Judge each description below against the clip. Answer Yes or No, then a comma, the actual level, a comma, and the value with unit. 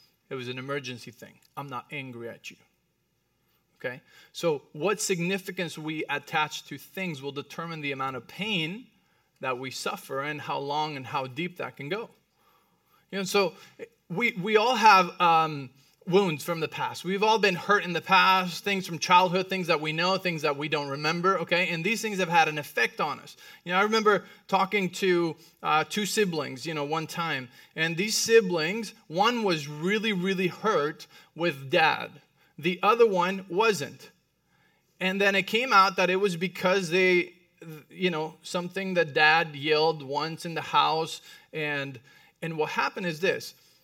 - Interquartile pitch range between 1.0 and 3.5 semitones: No, average, 4.0 semitones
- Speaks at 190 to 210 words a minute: No, average, 180 wpm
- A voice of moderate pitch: Yes, medium, 175 Hz